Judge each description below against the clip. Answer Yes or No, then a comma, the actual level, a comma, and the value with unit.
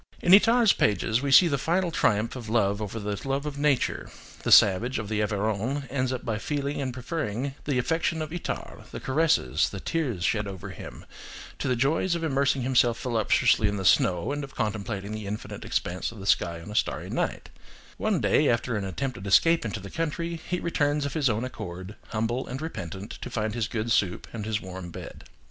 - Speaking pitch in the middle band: No, low, 120 Hz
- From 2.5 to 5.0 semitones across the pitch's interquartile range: No, wide, 5.6 semitones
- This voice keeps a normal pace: No, fast, 210 wpm